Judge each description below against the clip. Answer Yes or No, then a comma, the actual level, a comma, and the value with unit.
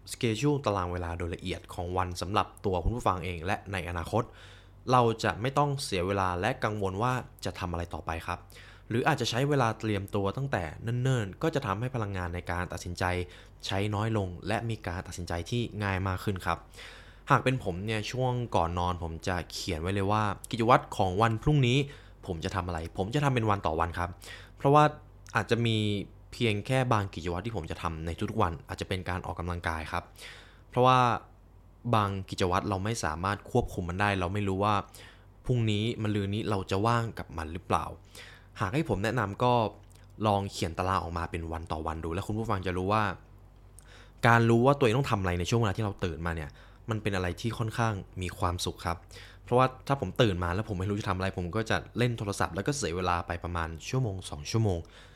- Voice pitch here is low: Yes, low, 100 Hz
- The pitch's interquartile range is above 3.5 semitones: Yes, average, 3.9 semitones